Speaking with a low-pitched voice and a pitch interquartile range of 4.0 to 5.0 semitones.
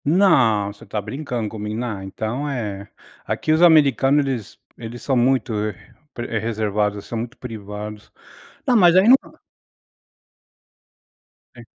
Yes: low, 115 Hz; average, 4.6 semitones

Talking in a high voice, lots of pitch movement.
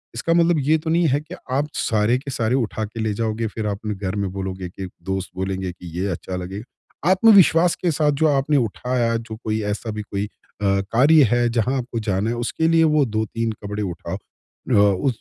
No: low, 115 Hz; wide, 5.7 semitones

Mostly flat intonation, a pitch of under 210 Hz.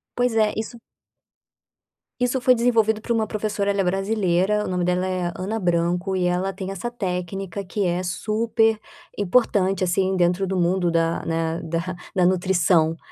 No: average, 3.1 semitones; high, 190 Hz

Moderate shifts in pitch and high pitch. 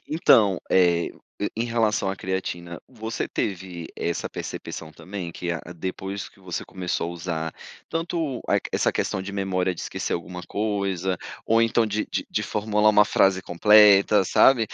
No: average, 3.2 semitones; very low, 95 Hz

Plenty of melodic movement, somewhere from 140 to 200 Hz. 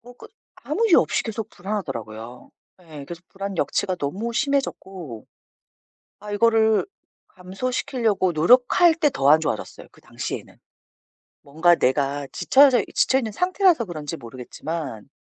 Yes: wide, 8.8 semitones; high, 190 Hz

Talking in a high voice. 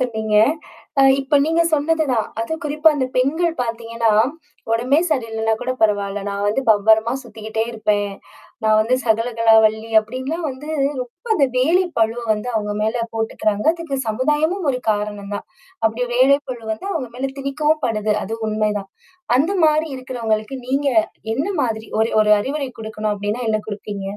Yes: high, 230 Hz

